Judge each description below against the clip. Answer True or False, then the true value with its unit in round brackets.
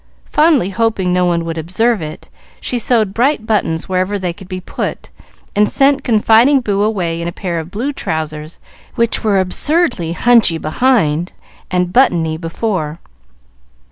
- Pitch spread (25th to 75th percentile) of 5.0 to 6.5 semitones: True (5.4 semitones)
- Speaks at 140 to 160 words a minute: True (150 wpm)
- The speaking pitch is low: False (190 Hz)